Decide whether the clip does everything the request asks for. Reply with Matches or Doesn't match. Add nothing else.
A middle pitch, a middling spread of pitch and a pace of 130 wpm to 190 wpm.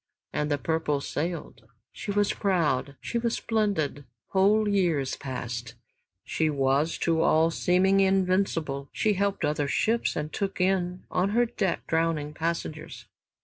Matches